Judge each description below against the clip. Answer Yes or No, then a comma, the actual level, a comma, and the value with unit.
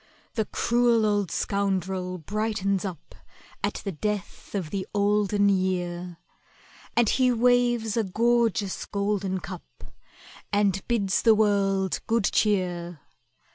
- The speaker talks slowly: Yes, slow, 115 wpm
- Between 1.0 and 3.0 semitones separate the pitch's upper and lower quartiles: Yes, narrow, 2.6 semitones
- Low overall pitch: No, high, 200 Hz